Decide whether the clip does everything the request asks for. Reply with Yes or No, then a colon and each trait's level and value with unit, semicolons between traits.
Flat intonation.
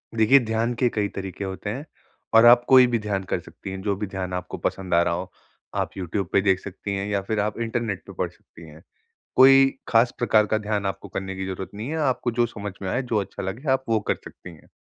No: average, 3.4 semitones